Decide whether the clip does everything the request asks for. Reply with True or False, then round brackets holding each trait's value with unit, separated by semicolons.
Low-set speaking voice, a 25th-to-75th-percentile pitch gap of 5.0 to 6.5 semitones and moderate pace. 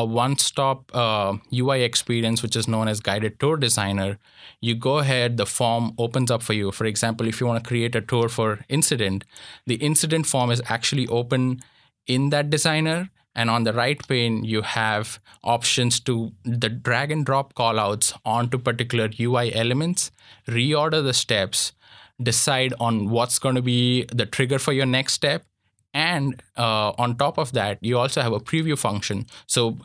False (120 Hz; 3.0 semitones; 175 wpm)